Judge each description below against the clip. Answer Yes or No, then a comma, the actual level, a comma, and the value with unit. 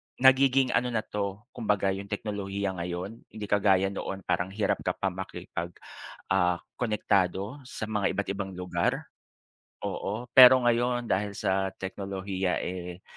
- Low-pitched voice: Yes, low, 100 Hz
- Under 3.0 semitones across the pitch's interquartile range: Yes, narrow, 2.5 semitones